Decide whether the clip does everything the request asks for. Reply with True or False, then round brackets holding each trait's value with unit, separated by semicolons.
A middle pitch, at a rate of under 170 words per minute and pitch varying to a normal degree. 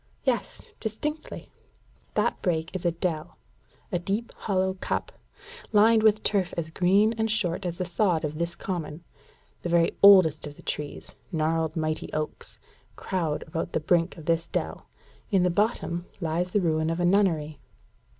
True (175 Hz; 160 wpm; 3.4 semitones)